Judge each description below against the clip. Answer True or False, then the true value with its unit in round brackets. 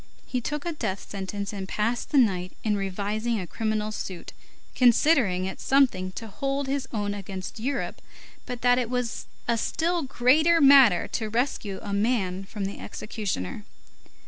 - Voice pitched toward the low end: False (220 Hz)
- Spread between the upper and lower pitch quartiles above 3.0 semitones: True (4.6 semitones)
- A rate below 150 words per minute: False (160 wpm)